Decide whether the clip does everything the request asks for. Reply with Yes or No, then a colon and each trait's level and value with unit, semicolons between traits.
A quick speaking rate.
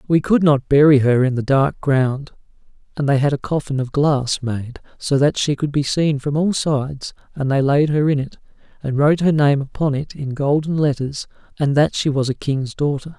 Yes: fast, 220 wpm